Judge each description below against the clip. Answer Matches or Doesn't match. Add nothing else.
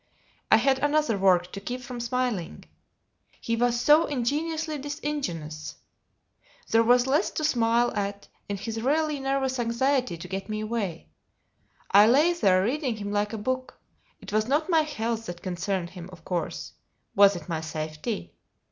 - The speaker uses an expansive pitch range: Matches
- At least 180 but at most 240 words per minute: Doesn't match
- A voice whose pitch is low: Doesn't match